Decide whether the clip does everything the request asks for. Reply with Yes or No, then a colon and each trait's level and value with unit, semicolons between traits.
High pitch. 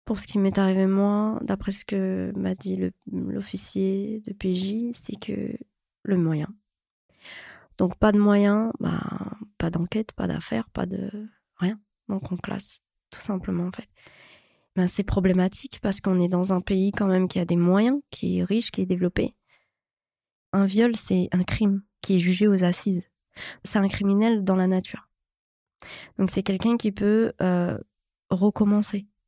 Yes: high, 195 Hz